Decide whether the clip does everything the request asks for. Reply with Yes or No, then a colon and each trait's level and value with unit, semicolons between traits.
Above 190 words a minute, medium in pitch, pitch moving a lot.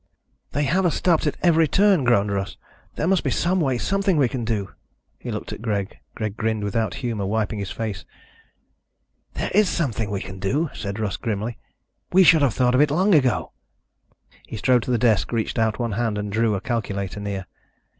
No: average, 200 wpm; low, 115 Hz; wide, 6.2 semitones